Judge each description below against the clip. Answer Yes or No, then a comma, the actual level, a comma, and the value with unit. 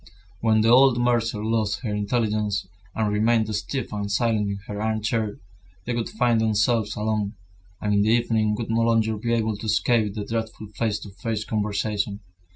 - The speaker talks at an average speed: Yes, average, 175 wpm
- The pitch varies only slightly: Yes, narrow, 1.6 semitones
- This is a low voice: Yes, low, 110 Hz